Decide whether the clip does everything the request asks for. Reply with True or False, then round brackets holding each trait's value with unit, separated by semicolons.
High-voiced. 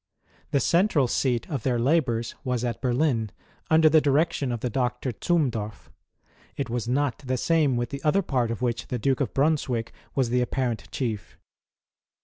False (125 Hz)